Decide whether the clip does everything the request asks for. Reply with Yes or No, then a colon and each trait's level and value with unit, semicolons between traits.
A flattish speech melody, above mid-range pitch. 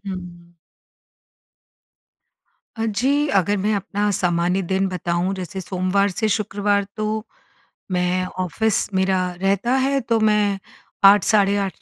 Yes: narrow, 2.3 semitones; high, 195 Hz